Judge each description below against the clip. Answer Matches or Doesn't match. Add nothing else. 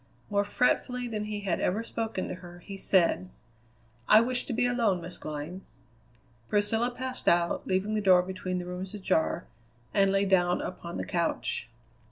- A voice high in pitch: Matches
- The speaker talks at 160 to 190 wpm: Matches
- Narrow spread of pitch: Doesn't match